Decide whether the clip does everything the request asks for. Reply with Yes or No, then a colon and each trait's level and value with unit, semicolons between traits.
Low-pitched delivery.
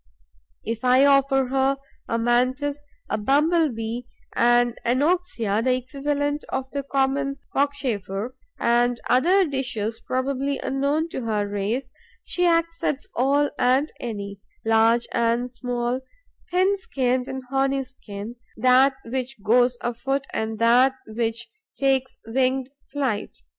No: very high, 255 Hz